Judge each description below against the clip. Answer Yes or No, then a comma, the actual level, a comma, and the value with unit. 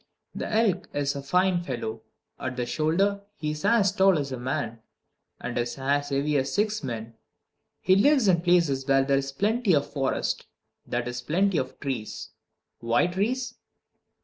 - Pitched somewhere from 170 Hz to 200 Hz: No, medium, 145 Hz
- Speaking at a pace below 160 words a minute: No, average, 170 wpm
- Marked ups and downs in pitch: Yes, wide, 6.4 semitones